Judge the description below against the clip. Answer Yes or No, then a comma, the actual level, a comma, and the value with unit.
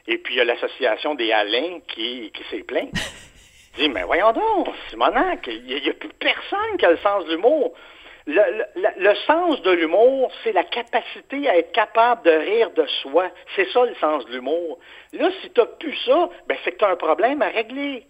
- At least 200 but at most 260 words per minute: Yes, fast, 220 wpm